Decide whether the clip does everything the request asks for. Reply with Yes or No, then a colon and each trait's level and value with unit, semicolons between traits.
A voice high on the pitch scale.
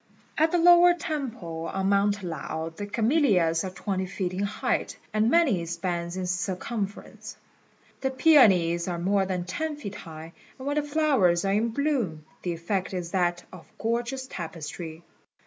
Yes: high, 195 Hz